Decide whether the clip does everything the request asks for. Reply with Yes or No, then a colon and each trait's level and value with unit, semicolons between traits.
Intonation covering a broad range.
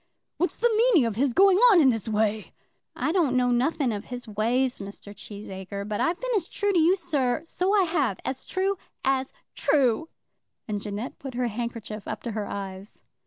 Yes: wide, 7.8 semitones